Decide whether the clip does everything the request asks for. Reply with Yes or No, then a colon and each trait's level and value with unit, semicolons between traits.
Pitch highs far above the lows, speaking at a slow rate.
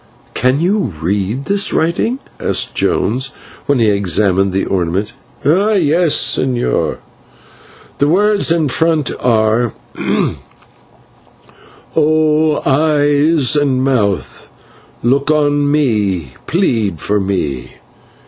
Yes: wide, 7.2 semitones; slow, 100 wpm